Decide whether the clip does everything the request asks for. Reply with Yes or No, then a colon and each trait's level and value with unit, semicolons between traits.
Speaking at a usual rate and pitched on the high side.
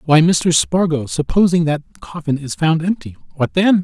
No: average, 155 wpm; medium, 160 Hz